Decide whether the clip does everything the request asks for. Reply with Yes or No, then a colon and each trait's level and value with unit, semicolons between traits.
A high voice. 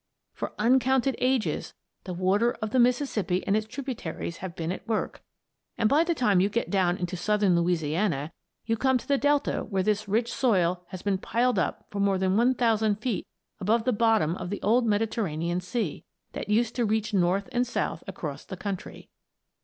Yes: high, 210 Hz